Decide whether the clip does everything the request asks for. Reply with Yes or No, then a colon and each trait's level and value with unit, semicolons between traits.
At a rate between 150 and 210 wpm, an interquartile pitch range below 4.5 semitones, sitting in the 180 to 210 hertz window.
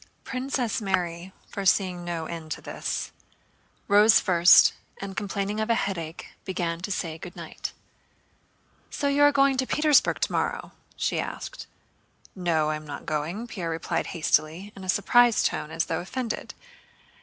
No: average, 155 wpm; average, 5.0 semitones; high, 190 Hz